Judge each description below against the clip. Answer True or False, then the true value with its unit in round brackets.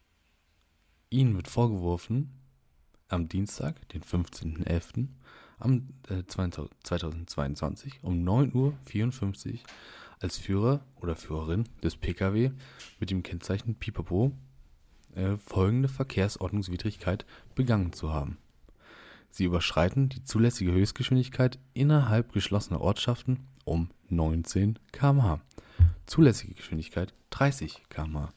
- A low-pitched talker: True (100 Hz)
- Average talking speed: False (85 wpm)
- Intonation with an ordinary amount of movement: False (6.5 semitones)